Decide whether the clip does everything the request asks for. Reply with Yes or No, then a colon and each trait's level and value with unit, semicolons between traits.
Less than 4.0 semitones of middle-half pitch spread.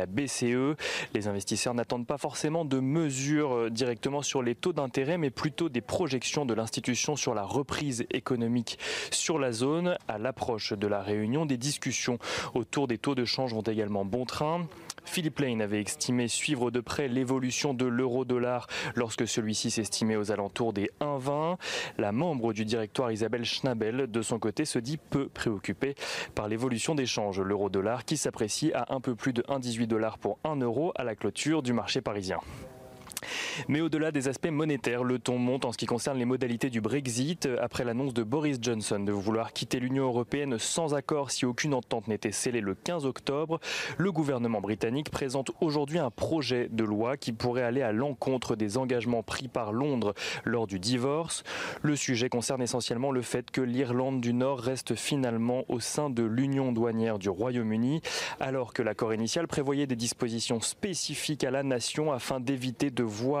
Yes: average, 3.5 semitones